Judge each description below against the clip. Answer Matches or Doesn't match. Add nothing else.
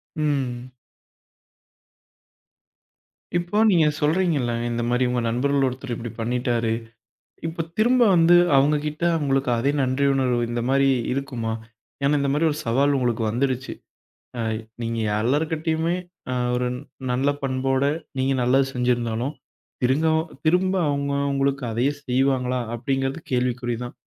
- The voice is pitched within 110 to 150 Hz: Matches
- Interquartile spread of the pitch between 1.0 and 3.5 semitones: Matches